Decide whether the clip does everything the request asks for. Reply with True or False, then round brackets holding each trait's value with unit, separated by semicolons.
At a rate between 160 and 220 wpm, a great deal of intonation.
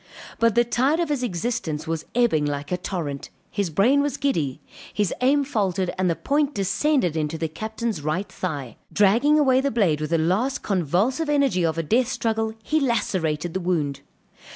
True (180 wpm; 7.7 semitones)